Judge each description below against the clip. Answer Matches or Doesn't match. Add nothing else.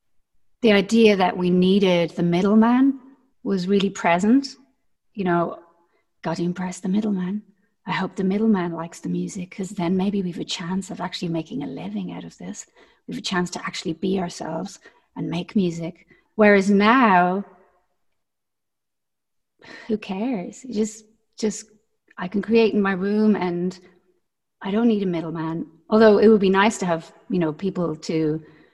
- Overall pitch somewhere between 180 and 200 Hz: Matches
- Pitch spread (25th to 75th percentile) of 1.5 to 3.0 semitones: Doesn't match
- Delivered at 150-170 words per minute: Matches